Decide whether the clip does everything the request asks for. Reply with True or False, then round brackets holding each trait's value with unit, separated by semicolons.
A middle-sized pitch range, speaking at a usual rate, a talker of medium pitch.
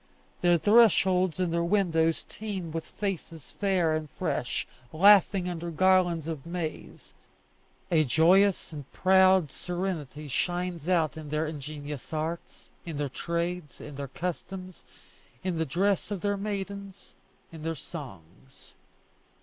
False (3.3 semitones; 130 wpm; 170 Hz)